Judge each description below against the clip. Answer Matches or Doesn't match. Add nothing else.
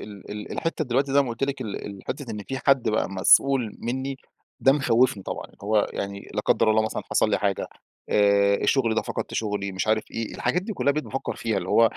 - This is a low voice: Matches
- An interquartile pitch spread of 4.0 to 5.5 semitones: Matches